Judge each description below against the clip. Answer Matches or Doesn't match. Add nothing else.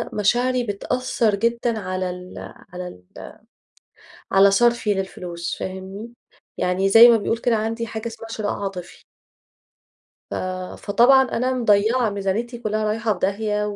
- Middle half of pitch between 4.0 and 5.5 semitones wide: Doesn't match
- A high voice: Matches